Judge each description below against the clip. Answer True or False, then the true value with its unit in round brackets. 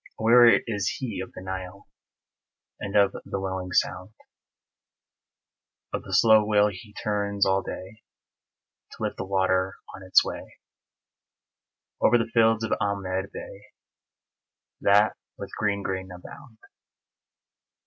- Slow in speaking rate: True (125 wpm)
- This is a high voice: False (100 Hz)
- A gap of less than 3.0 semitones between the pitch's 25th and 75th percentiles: True (2.5 semitones)